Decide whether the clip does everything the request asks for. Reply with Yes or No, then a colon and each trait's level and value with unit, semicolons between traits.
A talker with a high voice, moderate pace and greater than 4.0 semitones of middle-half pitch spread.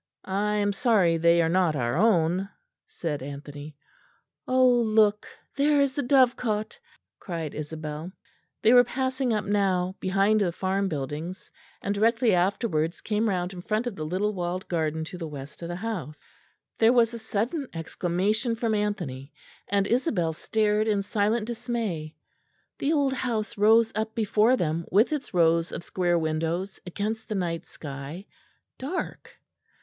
Yes: high, 200 Hz; average, 155 wpm; average, 5.1 semitones